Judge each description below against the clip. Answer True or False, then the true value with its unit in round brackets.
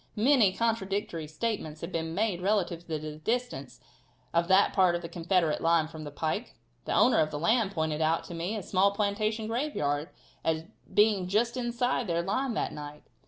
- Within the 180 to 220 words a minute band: True (185 wpm)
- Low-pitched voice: False (185 Hz)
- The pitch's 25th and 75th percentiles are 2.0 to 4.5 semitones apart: False (5.2 semitones)